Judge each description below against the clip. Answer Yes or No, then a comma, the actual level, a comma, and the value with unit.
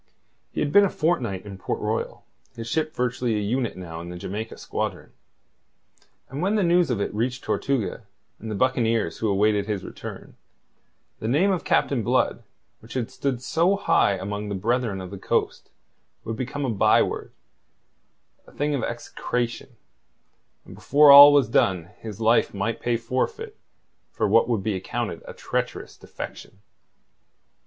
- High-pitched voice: No, low, 115 Hz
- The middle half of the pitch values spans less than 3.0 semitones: No, average, 5.2 semitones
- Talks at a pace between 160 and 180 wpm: Yes, average, 165 wpm